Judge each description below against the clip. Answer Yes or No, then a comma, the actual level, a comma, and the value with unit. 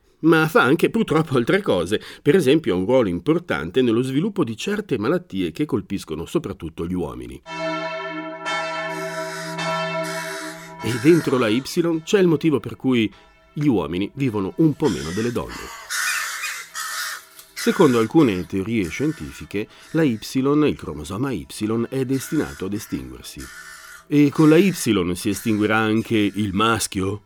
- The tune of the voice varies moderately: No, wide, 7.6 semitones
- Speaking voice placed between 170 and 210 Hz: No, low, 135 Hz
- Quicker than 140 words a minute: No, average, 135 wpm